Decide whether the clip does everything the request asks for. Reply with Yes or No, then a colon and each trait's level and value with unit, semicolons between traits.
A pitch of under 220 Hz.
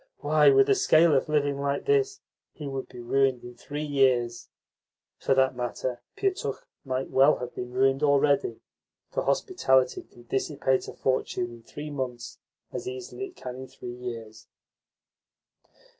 Yes: low, 135 Hz